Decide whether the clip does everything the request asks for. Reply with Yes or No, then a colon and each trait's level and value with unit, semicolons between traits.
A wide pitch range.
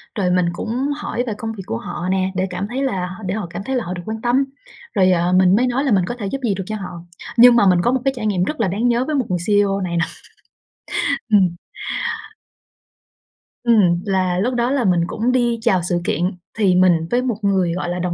No: average, 4.8 semitones